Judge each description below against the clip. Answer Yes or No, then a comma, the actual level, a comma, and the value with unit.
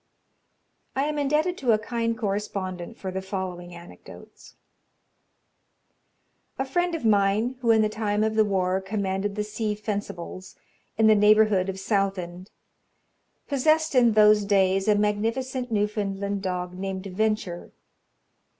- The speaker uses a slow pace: Yes, slow, 130 wpm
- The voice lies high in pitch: Yes, high, 210 Hz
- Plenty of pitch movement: No, average, 2.9 semitones